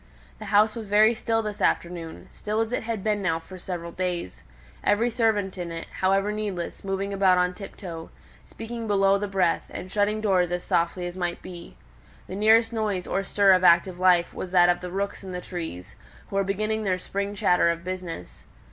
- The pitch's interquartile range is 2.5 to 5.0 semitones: Yes, average, 2.8 semitones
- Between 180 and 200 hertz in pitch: Yes, high, 190 Hz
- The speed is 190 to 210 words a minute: Yes, average, 200 wpm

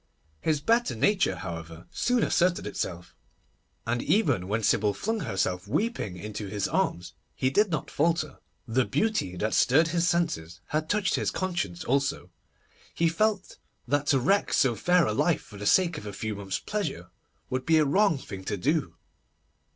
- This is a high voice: No, medium, 140 Hz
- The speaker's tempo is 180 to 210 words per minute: No, average, 170 wpm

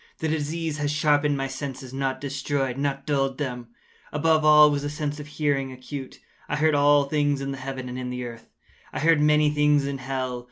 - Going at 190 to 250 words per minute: Yes, average, 195 wpm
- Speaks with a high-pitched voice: No, medium, 145 Hz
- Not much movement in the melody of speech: Yes, narrow, 1.8 semitones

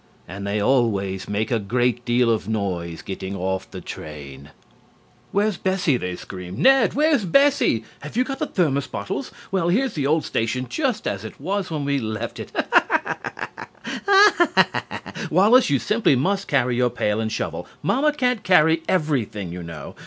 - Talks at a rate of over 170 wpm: No, average, 165 wpm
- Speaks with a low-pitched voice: Yes, low, 130 Hz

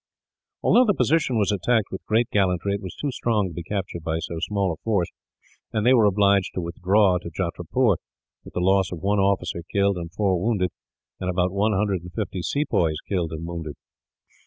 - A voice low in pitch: Yes, very low, 95 Hz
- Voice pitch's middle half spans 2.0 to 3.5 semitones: Yes, average, 3.2 semitones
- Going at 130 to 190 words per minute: No, average, 200 wpm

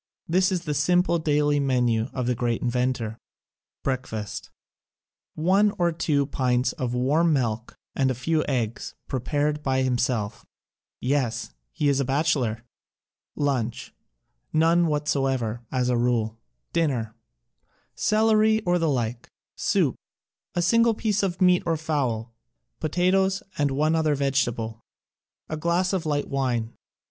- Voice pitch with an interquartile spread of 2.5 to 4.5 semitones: No, average, 5.1 semitones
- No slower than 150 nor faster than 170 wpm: No, slow, 135 wpm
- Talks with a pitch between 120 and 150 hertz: Yes, medium, 140 Hz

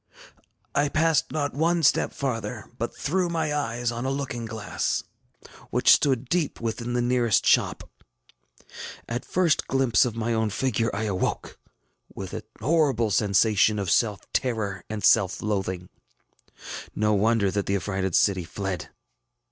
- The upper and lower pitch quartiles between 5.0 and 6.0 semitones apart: No, average, 4.6 semitones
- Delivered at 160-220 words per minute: No, average, 145 wpm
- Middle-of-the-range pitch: No, low, 115 Hz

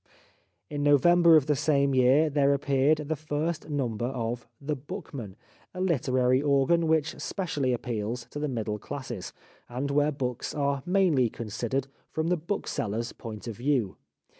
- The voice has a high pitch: No, medium, 140 Hz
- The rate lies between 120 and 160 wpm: Yes, average, 150 wpm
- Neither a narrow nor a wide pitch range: Yes, average, 3.7 semitones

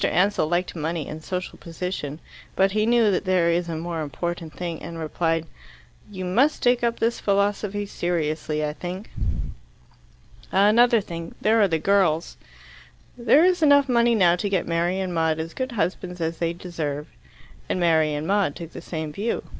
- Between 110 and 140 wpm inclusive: No, average, 175 wpm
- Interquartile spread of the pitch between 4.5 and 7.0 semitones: No, average, 4.0 semitones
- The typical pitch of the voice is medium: Yes, medium, 180 Hz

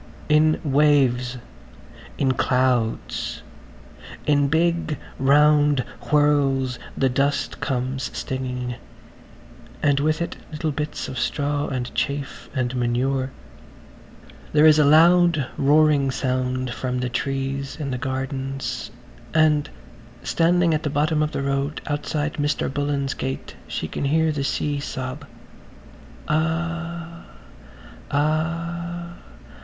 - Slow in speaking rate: Yes, slow, 110 wpm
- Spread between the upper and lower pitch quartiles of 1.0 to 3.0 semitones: Yes, narrow, 2.6 semitones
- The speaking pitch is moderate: Yes, medium, 145 Hz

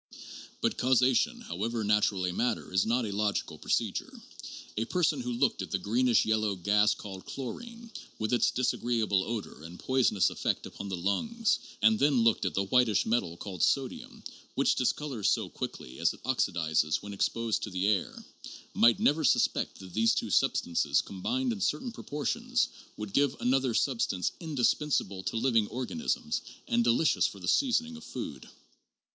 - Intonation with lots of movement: Yes, wide, 6.1 semitones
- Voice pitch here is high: No, low, 115 Hz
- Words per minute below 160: No, average, 165 wpm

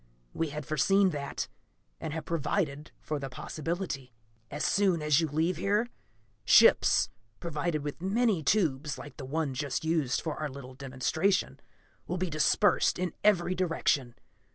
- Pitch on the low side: No, medium, 155 Hz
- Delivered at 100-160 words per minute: Yes, average, 150 wpm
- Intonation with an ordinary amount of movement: Yes, average, 4.0 semitones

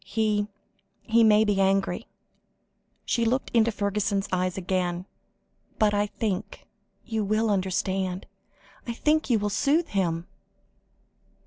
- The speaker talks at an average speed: No, slow, 120 wpm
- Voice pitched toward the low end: No, high, 205 Hz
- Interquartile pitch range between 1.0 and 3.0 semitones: Yes, narrow, 2.6 semitones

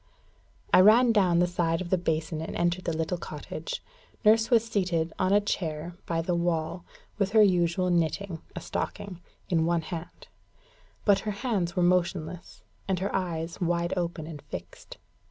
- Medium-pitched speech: Yes, medium, 175 Hz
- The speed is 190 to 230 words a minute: No, average, 170 wpm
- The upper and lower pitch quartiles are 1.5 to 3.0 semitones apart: Yes, narrow, 2.4 semitones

